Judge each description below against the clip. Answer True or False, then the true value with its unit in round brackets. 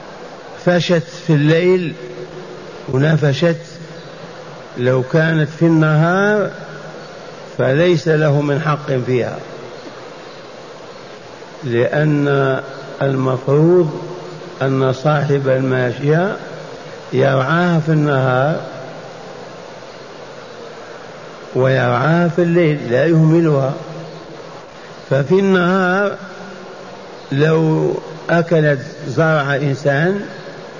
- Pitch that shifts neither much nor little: True (4.2 semitones)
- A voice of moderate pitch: True (160 Hz)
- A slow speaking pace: True (60 wpm)